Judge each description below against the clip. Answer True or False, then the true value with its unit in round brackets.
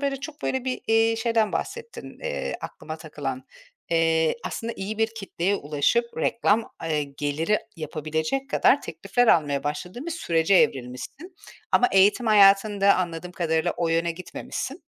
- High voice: True (195 Hz)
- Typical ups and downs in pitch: False (6.2 semitones)